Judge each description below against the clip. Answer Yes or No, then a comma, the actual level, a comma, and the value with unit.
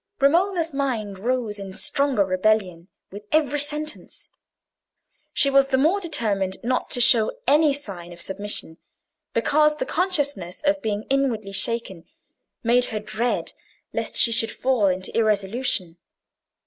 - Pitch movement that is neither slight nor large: No, wide, 6.2 semitones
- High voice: Yes, high, 235 Hz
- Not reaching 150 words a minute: Yes, slow, 135 wpm